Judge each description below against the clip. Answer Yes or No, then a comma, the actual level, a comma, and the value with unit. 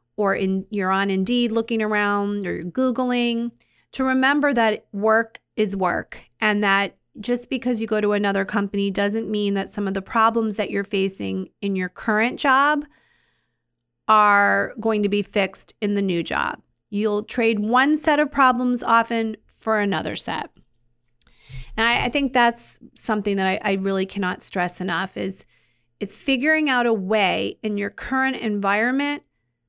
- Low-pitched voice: No, high, 210 Hz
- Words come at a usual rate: Yes, average, 165 wpm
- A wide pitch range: No, average, 3.4 semitones